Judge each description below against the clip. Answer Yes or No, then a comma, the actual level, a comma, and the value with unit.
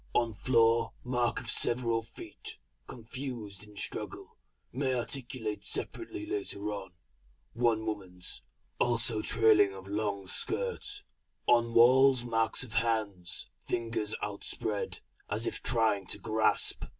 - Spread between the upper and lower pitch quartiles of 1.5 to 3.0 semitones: Yes, average, 2.7 semitones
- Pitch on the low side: Yes, low, 115 Hz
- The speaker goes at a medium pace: No, slow, 115 wpm